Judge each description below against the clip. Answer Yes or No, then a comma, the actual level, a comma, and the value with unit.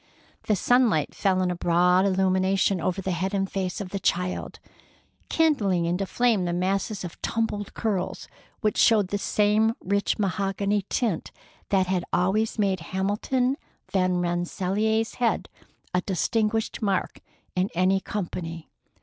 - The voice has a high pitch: Yes, high, 195 Hz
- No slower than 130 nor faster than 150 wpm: Yes, average, 140 wpm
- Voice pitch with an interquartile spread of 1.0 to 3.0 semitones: Yes, narrow, 2.6 semitones